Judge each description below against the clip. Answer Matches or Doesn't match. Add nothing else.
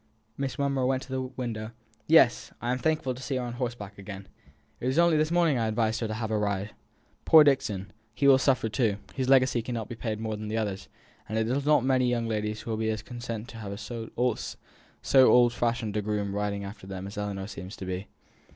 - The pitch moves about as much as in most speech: Matches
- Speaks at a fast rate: Matches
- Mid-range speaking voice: Doesn't match